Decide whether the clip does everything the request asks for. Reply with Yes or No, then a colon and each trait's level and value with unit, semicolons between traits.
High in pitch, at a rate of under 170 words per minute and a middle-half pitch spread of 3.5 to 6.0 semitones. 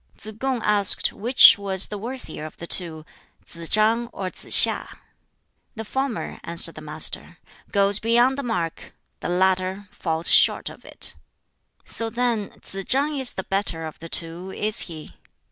Yes: high, 200 Hz; average, 160 wpm; average, 5.3 semitones